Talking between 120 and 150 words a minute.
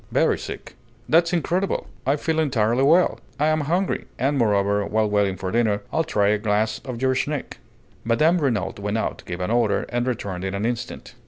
No: average, 185 wpm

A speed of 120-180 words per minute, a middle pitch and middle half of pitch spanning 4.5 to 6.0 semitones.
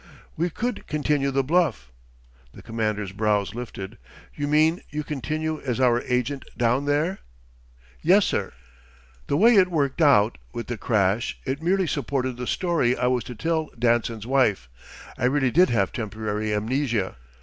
No: average, 155 wpm; low, 130 Hz; average, 5.2 semitones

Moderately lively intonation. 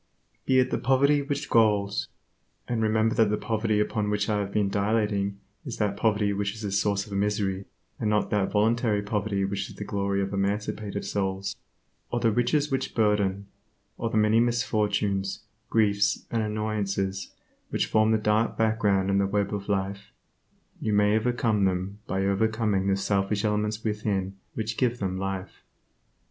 No: narrow, 1.8 semitones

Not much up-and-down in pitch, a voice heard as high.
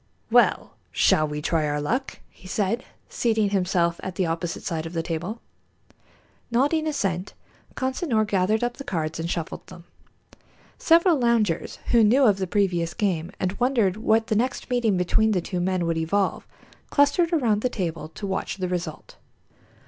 No: wide, 5.6 semitones; high, 195 Hz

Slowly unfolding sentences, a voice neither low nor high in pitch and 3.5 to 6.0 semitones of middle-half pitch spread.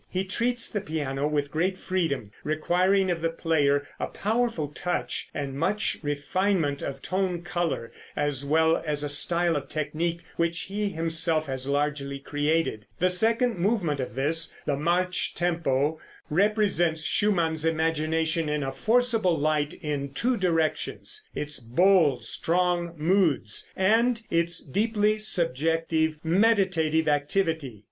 Yes: slow, 130 wpm; medium, 165 Hz; average, 4.1 semitones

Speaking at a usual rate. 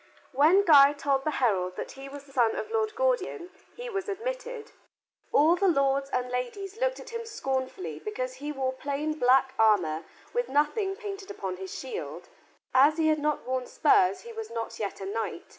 Yes: average, 190 wpm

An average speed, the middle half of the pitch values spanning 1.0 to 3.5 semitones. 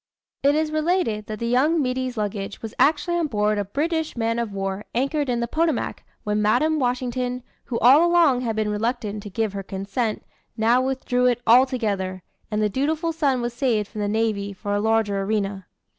No: average, 190 wpm; average, 4.3 semitones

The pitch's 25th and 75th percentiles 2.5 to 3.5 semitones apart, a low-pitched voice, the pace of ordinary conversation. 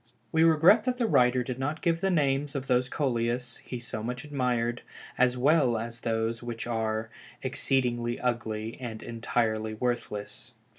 Yes: average, 2.8 semitones; low, 125 Hz; average, 155 wpm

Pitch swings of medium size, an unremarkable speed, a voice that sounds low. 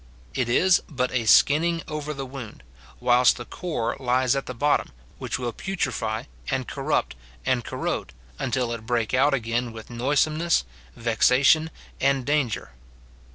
Yes: average, 3.7 semitones; average, 145 wpm; low, 130 Hz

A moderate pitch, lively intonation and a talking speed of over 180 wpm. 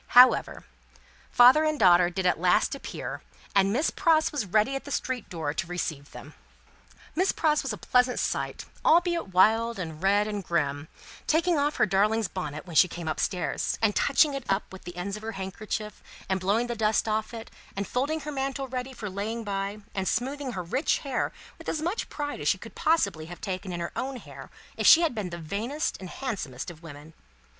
No: high, 215 Hz; wide, 6.8 semitones; fast, 205 wpm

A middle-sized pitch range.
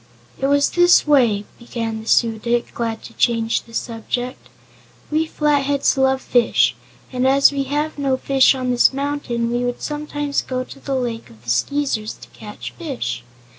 Yes: average, 3.6 semitones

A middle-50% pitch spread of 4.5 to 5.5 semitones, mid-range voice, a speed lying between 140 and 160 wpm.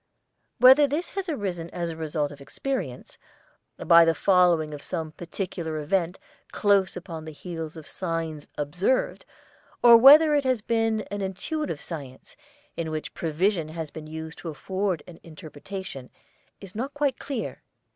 Yes: average, 5.2 semitones; medium, 175 Hz; average, 150 wpm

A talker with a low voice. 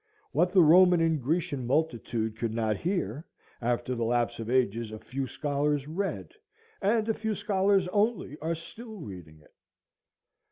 No: medium, 145 Hz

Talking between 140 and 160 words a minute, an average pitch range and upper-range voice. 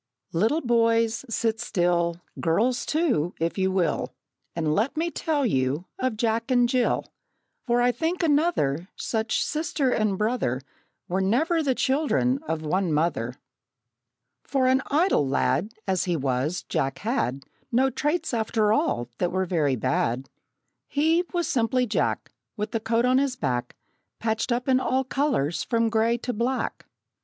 No: average, 150 wpm; wide, 7.2 semitones; high, 225 Hz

